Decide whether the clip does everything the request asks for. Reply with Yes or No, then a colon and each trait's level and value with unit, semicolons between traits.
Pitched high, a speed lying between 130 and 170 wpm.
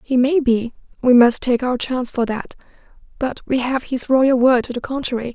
No: very high, 250 Hz; average, 200 wpm